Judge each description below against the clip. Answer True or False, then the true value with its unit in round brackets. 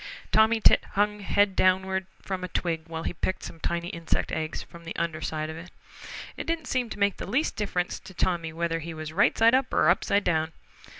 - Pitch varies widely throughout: False (3.6 semitones)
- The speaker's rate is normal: False (220 wpm)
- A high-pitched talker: False (180 Hz)